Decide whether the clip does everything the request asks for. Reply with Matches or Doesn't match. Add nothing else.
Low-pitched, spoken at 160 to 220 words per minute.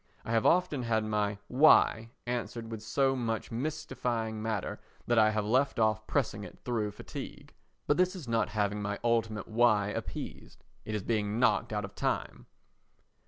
Matches